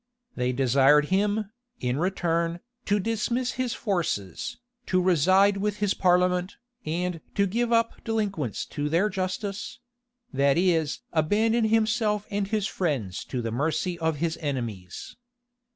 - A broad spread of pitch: Yes, wide, 5.8 semitones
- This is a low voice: No, medium, 180 Hz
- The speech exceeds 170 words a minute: No, slow, 135 wpm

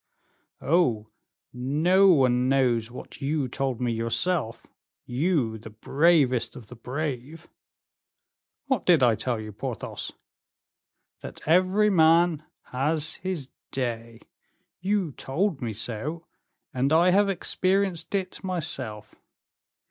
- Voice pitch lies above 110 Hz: Yes, medium, 140 Hz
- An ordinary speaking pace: No, slow, 110 wpm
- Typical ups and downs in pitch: No, wide, 6.2 semitones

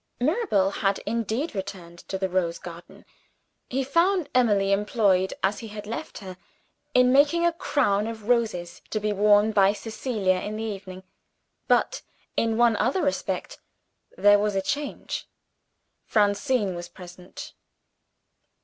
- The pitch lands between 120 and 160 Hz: No, high, 210 Hz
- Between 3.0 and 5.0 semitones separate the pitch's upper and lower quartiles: Yes, average, 4.1 semitones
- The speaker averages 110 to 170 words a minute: Yes, average, 140 wpm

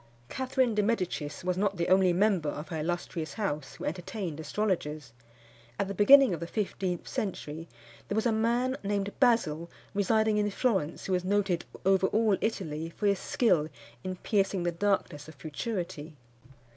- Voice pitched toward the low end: No, high, 190 Hz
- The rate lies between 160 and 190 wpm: Yes, average, 165 wpm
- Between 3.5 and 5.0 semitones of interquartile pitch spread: Yes, average, 4.1 semitones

